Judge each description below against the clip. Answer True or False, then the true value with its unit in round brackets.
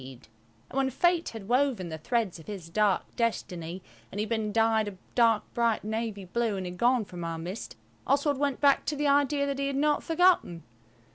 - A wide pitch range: True (6.5 semitones)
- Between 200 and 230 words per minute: True (205 wpm)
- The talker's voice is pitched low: False (225 Hz)